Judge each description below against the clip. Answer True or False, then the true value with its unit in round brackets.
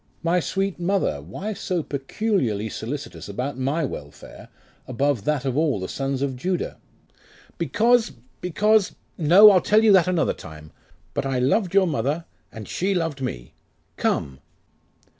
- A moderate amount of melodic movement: False (6.7 semitones)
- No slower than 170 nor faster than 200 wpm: False (145 wpm)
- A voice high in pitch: False (150 Hz)